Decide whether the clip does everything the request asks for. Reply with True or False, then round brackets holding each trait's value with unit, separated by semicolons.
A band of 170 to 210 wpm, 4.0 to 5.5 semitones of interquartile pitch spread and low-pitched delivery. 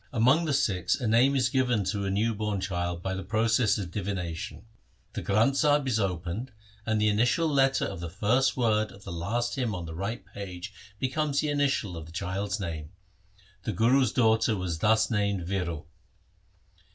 True (185 wpm; 4.9 semitones; 105 Hz)